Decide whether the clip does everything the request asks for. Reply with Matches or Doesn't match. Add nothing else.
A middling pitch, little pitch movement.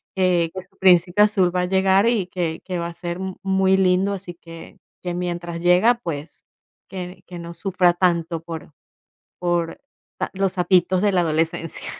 Matches